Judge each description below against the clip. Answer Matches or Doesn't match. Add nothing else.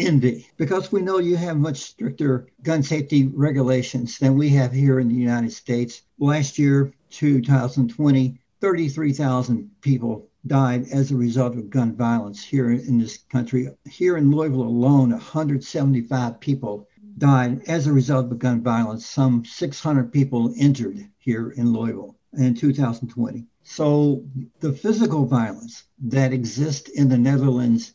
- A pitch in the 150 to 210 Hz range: Doesn't match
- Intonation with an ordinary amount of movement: Matches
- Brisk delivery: Doesn't match